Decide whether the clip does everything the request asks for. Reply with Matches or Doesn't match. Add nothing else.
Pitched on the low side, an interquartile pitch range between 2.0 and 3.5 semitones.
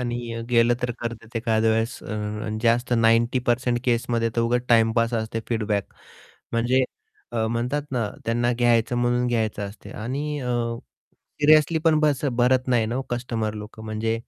Doesn't match